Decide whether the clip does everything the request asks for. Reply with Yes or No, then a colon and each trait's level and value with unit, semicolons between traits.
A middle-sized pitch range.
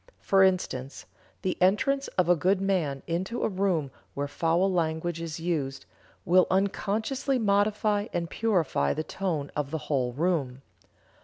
Yes: average, 4.2 semitones